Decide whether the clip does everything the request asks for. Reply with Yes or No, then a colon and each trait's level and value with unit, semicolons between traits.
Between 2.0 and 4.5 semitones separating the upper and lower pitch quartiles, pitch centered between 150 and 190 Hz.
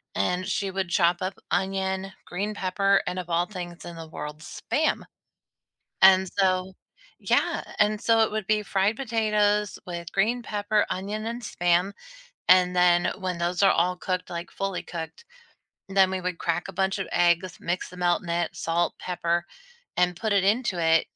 Yes: narrow, 2.4 semitones; medium, 185 Hz